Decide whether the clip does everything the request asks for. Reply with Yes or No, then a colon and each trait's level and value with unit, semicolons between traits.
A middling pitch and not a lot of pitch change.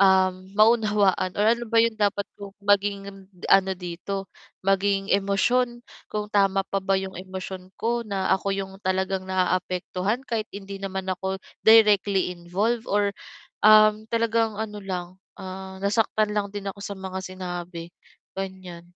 No: high, 195 Hz; narrow, 1.9 semitones